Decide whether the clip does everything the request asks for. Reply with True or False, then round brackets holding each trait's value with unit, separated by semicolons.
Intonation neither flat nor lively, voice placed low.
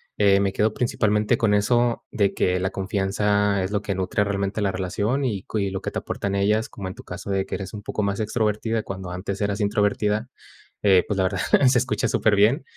False (1.7 semitones; 100 Hz)